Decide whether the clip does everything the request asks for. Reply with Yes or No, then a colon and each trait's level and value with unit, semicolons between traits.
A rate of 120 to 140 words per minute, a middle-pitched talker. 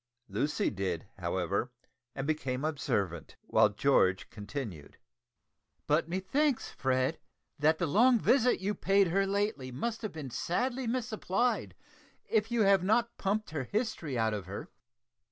Yes: slow, 135 wpm; medium, 165 Hz